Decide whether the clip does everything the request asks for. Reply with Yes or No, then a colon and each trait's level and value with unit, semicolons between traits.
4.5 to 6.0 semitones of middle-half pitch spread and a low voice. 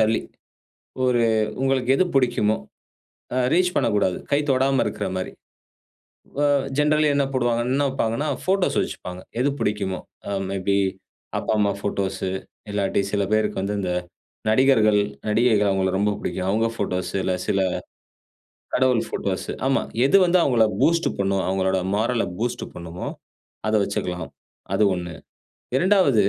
Yes: average, 5.2 semitones; low, 110 Hz